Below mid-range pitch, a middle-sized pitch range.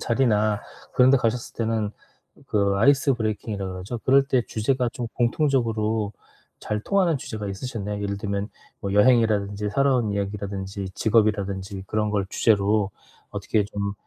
Yes: low, 105 Hz; average, 3.0 semitones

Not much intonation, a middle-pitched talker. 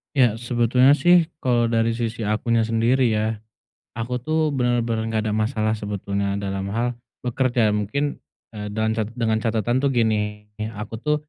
No: narrow, 2.3 semitones; low, 115 Hz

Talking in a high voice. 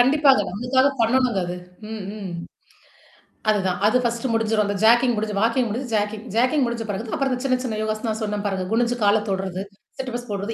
Yes: high, 225 Hz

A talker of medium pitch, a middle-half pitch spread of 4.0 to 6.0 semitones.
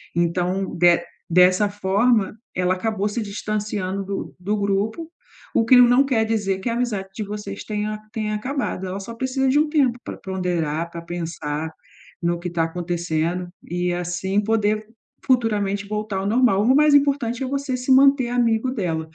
No: high, 205 Hz; average, 4.8 semitones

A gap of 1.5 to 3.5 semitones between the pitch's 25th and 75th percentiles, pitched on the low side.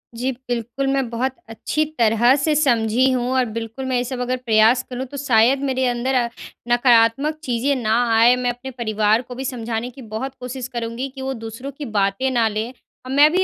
No: narrow, 2.5 semitones; high, 245 Hz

